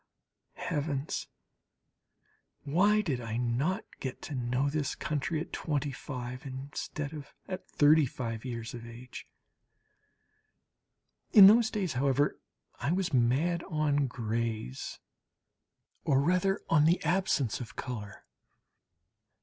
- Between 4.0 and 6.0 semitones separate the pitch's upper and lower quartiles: Yes, average, 4.7 semitones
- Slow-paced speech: Yes, slow, 110 wpm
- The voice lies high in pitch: No, medium, 140 Hz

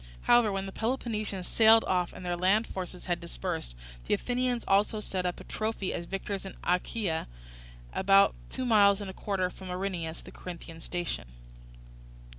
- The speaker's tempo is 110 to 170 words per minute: Yes, average, 165 wpm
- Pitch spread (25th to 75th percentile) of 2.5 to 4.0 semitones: Yes, average, 3.2 semitones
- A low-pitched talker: No, high, 195 Hz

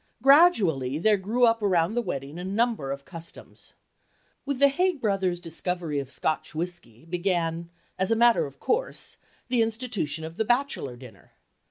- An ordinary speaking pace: Yes, average, 160 wpm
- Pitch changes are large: Yes, wide, 6.5 semitones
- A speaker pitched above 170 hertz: Yes, medium, 185 Hz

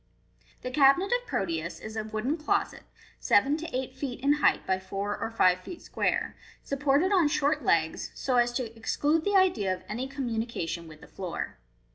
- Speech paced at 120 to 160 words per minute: No, average, 185 wpm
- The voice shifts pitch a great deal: Yes, wide, 6.4 semitones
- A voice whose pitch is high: Yes, very high, 255 Hz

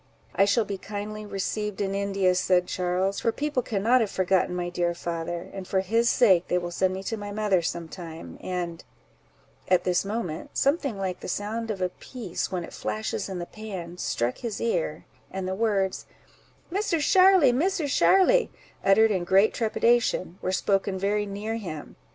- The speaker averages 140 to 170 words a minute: No, average, 180 wpm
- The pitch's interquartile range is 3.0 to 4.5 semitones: Yes, average, 3.5 semitones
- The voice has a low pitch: No, high, 195 Hz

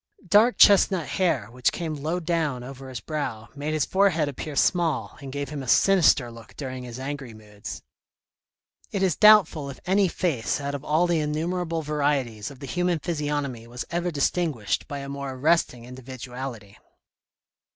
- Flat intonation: No, average, 4.7 semitones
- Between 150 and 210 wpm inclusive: Yes, average, 165 wpm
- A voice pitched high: No, medium, 145 Hz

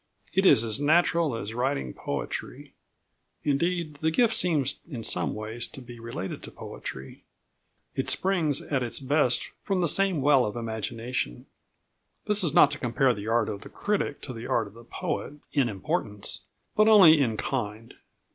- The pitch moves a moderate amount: No, wide, 5.9 semitones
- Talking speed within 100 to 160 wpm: No, average, 170 wpm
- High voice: No, low, 135 Hz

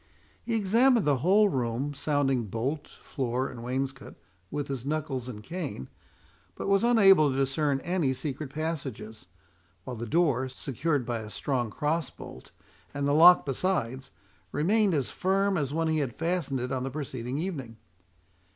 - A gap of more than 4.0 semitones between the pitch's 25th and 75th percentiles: Yes, average, 4.6 semitones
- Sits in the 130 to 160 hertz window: Yes, medium, 140 Hz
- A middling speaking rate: Yes, average, 160 wpm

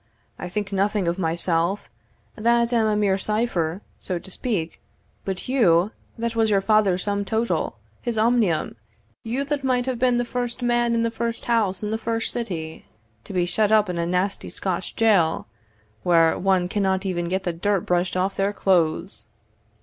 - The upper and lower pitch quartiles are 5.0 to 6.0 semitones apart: No, average, 4.3 semitones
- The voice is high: Yes, high, 200 Hz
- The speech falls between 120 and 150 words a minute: No, average, 180 wpm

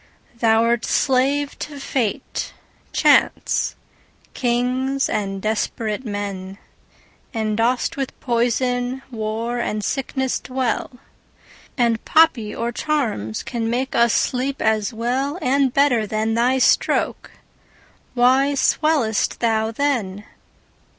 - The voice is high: Yes, high, 240 Hz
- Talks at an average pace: No, slow, 105 wpm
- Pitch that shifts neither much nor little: Yes, average, 3.2 semitones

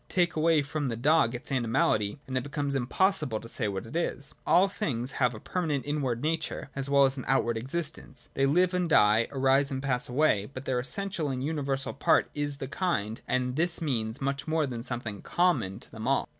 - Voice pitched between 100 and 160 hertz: Yes, low, 135 Hz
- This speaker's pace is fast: Yes, fast, 210 wpm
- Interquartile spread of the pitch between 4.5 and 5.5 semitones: No, average, 4.1 semitones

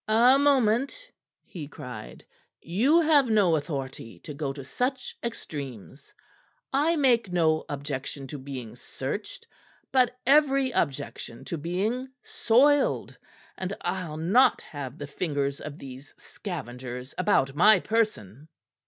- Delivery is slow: Yes, slow, 120 wpm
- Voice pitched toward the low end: No, medium, 170 Hz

